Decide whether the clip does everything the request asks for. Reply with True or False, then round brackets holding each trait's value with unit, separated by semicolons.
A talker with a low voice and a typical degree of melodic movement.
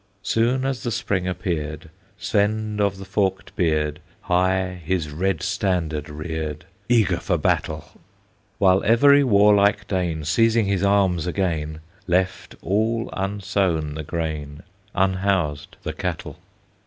True (95 Hz; 4.1 semitones)